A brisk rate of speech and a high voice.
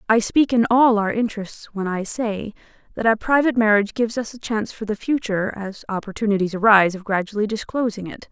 No: average, 195 wpm; high, 215 Hz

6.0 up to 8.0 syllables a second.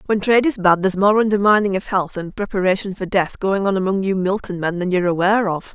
Yes: 6.4 syllables/s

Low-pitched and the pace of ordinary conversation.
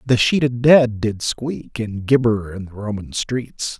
Yes: low, 115 Hz; average, 175 wpm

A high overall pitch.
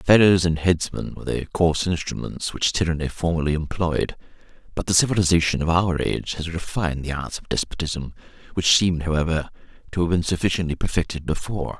No: very low, 85 Hz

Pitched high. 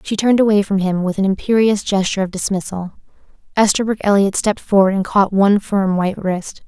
Yes: high, 200 Hz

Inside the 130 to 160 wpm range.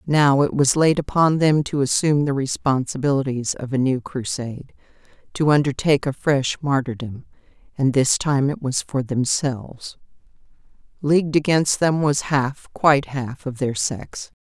Yes: average, 140 wpm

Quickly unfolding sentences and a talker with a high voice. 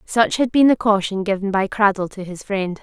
Yes: fast, 235 wpm; high, 205 Hz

